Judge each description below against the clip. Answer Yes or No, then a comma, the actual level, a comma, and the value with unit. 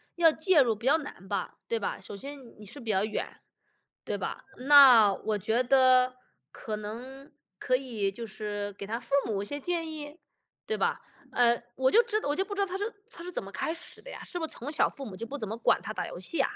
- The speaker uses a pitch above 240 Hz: Yes, very high, 255 Hz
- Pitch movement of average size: No, wide, 6.4 semitones